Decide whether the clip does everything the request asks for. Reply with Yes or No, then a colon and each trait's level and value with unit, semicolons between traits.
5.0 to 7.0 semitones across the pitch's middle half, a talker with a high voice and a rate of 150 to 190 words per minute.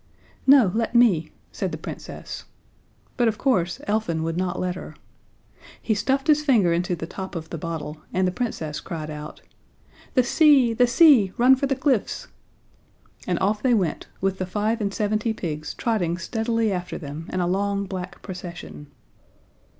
Yes: average, 5.3 semitones; high, 195 Hz; average, 170 wpm